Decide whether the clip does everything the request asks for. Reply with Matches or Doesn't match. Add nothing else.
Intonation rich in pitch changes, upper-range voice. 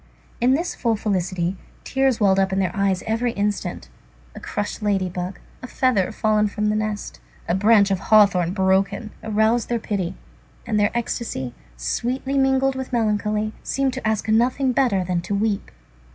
Doesn't match